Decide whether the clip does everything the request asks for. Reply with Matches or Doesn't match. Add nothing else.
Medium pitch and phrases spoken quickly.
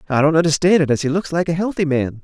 Matches